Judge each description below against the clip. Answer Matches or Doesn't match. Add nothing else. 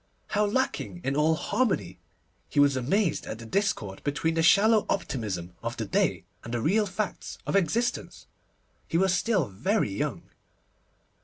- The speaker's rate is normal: Matches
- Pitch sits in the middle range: Matches